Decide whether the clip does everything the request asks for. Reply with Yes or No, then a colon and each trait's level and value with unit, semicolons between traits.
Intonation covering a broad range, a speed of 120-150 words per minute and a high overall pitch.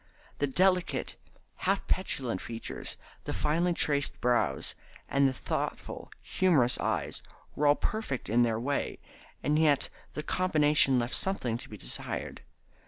No: wide, 5.8 semitones; slow, 135 wpm; medium, 145 Hz